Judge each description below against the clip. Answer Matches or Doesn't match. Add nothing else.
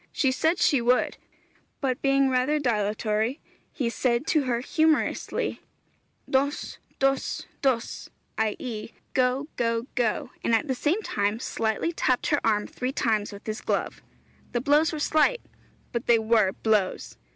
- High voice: Matches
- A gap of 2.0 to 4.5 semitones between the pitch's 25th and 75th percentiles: Matches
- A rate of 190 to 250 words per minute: Doesn't match